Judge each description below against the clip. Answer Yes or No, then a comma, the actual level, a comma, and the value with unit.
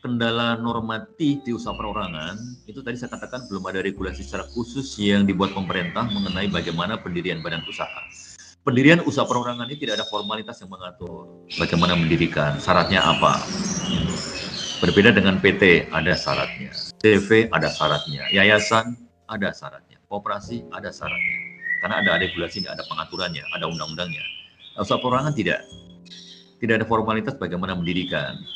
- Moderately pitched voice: No, low, 110 Hz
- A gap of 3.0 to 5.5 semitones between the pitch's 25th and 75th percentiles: Yes, average, 4.6 semitones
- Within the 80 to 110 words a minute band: No, average, 135 wpm